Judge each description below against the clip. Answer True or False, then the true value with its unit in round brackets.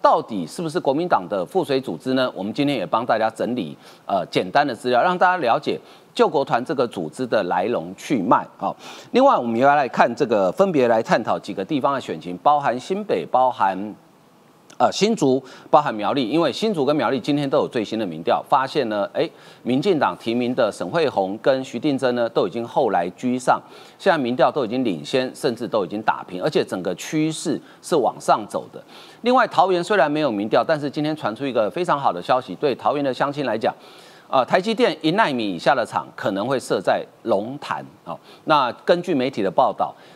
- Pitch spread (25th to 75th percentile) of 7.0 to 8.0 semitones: False (5.3 semitones)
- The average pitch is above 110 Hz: True (135 Hz)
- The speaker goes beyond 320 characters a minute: False (315 characters per minute)